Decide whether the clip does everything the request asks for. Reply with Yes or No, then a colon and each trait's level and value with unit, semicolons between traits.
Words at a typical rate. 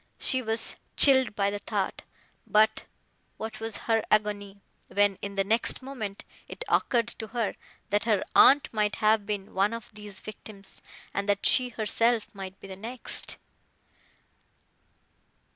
Yes: average, 145 wpm